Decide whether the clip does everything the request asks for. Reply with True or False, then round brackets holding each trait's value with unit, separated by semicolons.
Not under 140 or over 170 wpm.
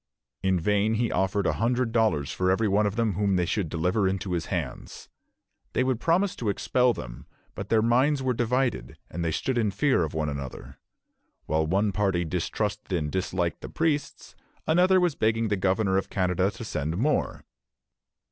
False (185 wpm)